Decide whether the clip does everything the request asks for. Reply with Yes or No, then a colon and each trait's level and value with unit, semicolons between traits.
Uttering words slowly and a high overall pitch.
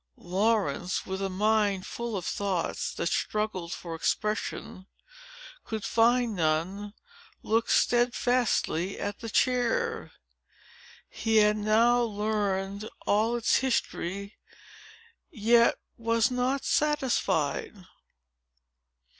Yes: slow, 95 wpm; high, 215 Hz